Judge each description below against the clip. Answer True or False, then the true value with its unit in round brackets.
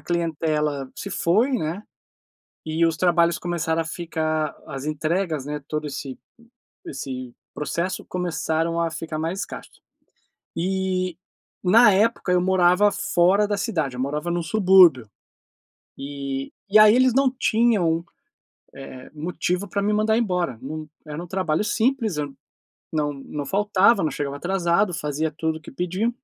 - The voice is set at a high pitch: False (170 Hz)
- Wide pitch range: False (4.1 semitones)